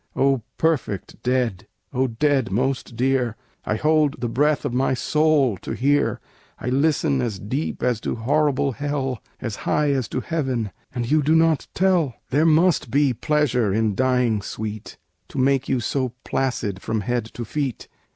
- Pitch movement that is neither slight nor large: Yes, average, 3.9 semitones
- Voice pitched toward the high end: No, low, 130 Hz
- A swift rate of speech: No, average, 165 wpm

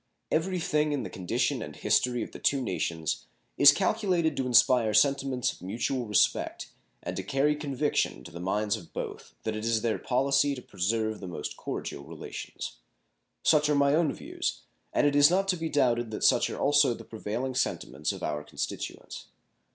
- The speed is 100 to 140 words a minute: No, average, 185 wpm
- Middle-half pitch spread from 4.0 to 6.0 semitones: Yes, average, 5.2 semitones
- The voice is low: Yes, low, 125 Hz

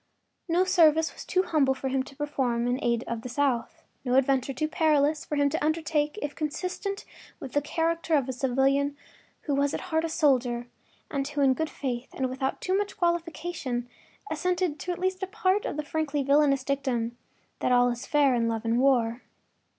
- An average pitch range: Yes, average, 3.8 semitones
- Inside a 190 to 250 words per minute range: Yes, average, 200 wpm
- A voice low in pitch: No, very high, 285 Hz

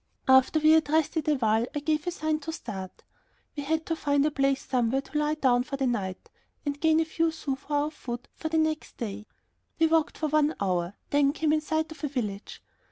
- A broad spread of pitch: No, average, 3.7 semitones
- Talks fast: Yes, fast, 230 wpm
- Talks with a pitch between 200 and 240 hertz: No, very high, 290 Hz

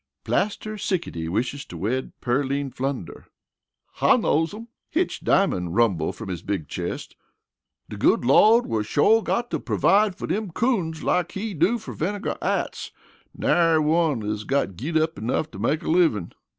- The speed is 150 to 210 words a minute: Yes, average, 165 wpm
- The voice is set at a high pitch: No, medium, 155 Hz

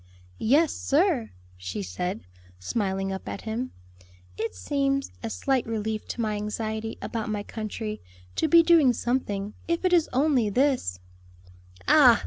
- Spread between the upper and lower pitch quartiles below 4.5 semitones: No, average, 4.9 semitones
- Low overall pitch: No, high, 225 Hz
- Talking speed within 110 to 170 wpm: Yes, average, 140 wpm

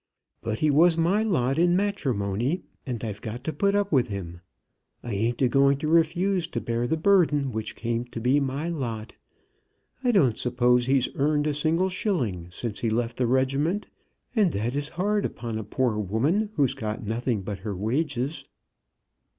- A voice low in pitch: Yes, low, 130 Hz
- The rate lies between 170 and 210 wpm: Yes, average, 180 wpm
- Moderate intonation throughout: No, wide, 6.2 semitones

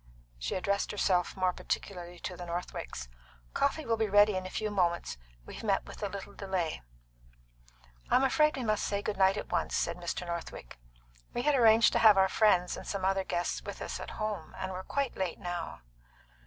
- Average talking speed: Yes, average, 195 wpm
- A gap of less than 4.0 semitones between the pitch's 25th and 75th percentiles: Yes, average, 3.3 semitones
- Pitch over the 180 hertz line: Yes, high, 190 Hz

